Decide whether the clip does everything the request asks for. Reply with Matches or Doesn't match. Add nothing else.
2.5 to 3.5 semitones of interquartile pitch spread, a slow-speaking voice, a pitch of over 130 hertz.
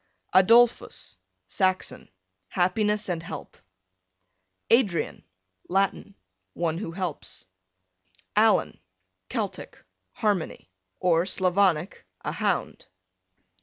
Matches